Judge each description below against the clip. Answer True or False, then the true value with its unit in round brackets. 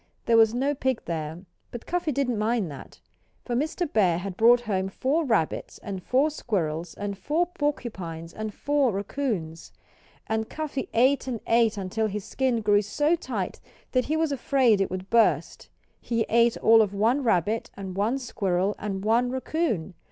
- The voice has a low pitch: False (225 Hz)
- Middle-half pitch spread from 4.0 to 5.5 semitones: True (5.1 semitones)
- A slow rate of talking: False (170 wpm)